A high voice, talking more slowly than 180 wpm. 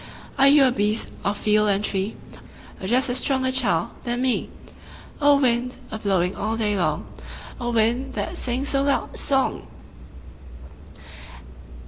Yes: high, 240 Hz; average, 150 wpm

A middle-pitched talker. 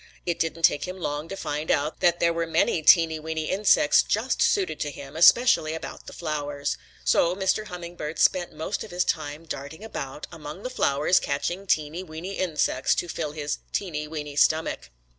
Yes: medium, 160 Hz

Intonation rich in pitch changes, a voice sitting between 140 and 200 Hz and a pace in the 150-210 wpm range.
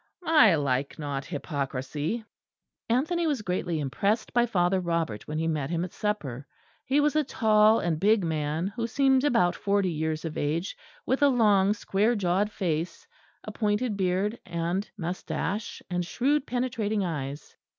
Yes: wide, 5.9 semitones; high, 190 Hz; average, 155 wpm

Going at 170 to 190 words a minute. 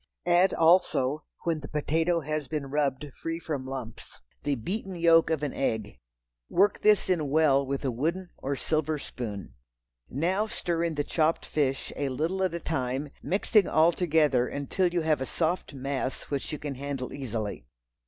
Yes: average, 175 wpm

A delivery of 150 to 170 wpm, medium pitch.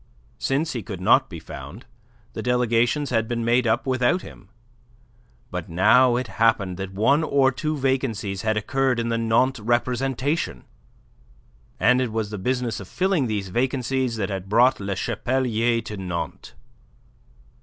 No: average, 155 wpm; low, 120 Hz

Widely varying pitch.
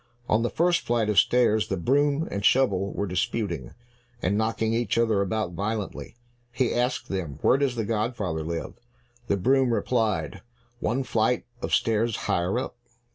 No: average, 3.7 semitones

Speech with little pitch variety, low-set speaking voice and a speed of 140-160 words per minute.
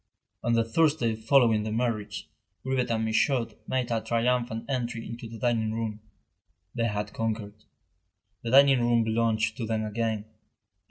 Yes: narrow, 1.6 semitones; low, 115 Hz; average, 150 wpm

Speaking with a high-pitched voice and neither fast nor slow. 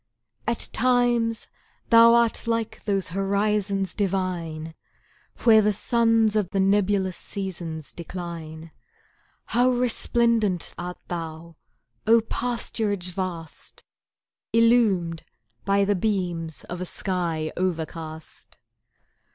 No: high, 195 Hz; slow, 95 wpm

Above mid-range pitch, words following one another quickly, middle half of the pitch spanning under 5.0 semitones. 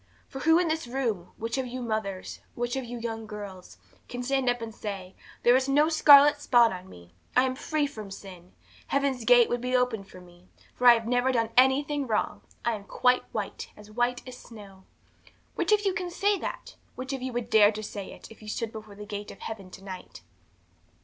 Yes: high, 240 Hz; fast, 220 wpm; average, 4.0 semitones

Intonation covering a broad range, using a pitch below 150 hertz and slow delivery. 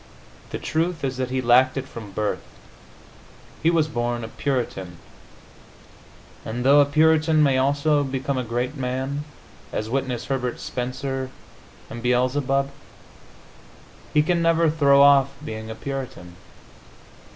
No: average, 2.7 semitones; low, 135 Hz; slow, 130 wpm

